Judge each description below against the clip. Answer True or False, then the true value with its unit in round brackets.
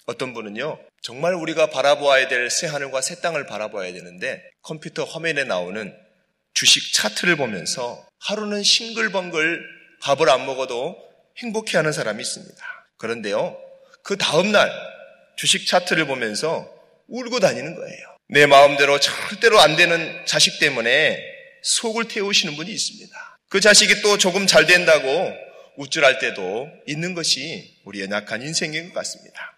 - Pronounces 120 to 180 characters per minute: False (320 characters per minute)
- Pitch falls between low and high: True (180 Hz)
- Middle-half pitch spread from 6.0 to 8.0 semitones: True (7.1 semitones)